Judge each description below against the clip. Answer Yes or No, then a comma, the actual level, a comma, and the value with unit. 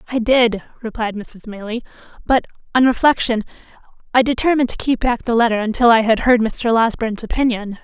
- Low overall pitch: No, high, 230 Hz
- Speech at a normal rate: Yes, average, 170 wpm